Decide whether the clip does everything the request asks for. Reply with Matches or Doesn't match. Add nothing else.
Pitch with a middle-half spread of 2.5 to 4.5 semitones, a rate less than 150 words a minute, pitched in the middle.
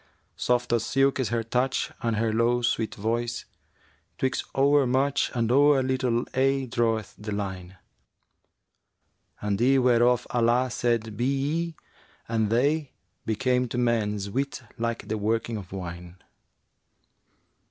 Doesn't match